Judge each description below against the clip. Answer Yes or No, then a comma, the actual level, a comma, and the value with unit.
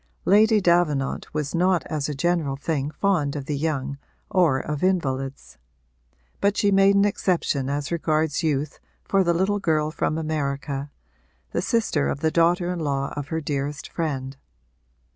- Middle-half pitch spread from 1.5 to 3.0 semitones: No, average, 3.9 semitones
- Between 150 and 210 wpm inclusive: Yes, average, 160 wpm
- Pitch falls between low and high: Yes, medium, 155 Hz